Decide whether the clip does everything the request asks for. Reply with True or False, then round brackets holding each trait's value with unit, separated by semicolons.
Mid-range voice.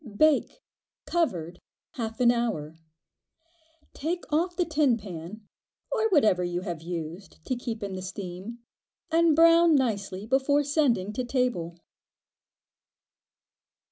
False (235 Hz)